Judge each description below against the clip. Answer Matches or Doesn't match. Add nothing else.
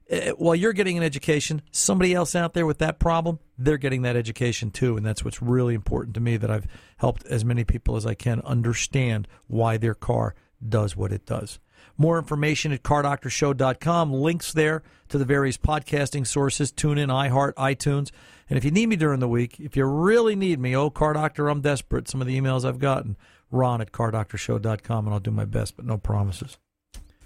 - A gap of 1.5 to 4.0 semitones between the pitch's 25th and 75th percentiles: Doesn't match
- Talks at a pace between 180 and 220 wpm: Matches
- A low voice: Matches